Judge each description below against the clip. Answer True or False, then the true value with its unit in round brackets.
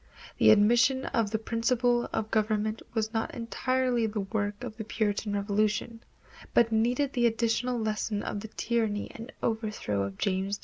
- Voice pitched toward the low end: False (220 Hz)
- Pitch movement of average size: False (2.1 semitones)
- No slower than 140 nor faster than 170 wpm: True (165 wpm)